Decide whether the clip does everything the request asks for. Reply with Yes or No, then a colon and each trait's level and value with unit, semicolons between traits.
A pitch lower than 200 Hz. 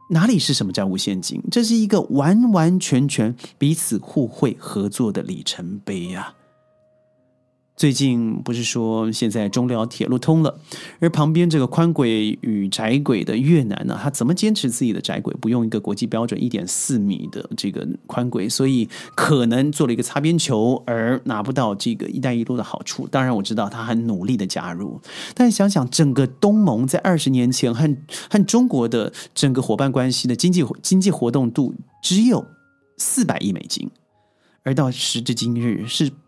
Yes: low, 135 Hz